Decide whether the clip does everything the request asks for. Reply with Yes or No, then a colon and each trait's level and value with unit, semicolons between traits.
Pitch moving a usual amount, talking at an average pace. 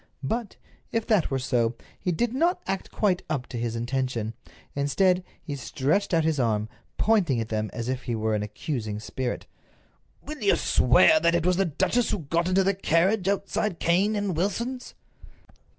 No: wide, 8.0 semitones; average, 180 wpm